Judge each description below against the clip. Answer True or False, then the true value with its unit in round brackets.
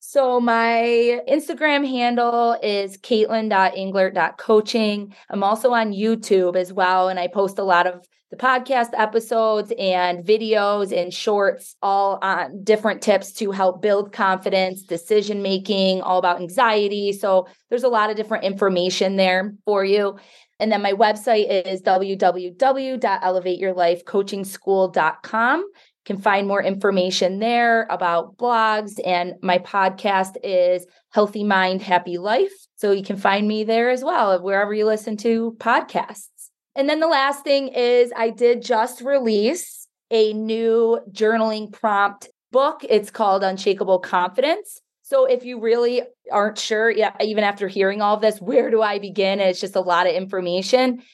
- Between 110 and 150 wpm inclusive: True (145 wpm)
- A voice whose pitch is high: True (210 Hz)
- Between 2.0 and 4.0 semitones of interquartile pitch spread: True (3.4 semitones)